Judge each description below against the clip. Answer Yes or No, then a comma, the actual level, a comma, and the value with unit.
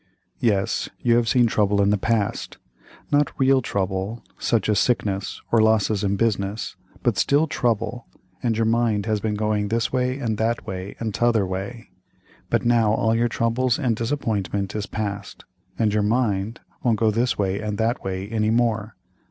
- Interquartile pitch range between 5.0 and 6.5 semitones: No, narrow, 2.5 semitones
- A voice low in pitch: Yes, low, 110 Hz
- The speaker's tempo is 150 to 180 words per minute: Yes, average, 175 wpm